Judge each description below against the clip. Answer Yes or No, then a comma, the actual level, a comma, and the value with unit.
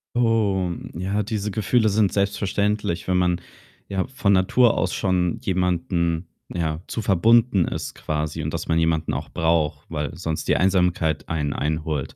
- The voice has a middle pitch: No, very low, 90 Hz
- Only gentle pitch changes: No, average, 3.7 semitones